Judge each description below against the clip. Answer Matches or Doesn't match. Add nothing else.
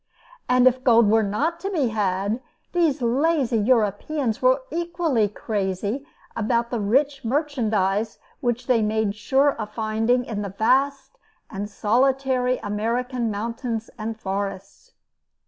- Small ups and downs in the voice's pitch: Doesn't match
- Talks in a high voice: Matches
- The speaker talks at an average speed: Doesn't match